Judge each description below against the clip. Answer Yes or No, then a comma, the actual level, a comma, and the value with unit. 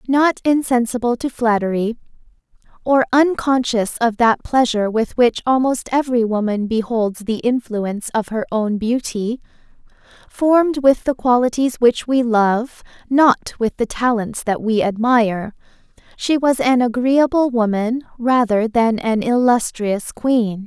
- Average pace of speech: No, slow, 130 wpm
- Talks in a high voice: Yes, high, 235 Hz